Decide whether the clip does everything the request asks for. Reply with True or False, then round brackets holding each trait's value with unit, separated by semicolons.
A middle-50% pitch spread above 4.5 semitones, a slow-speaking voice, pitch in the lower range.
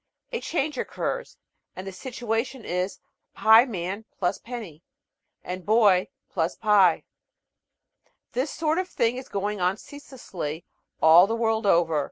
False (5.4 semitones; 130 wpm; 215 Hz)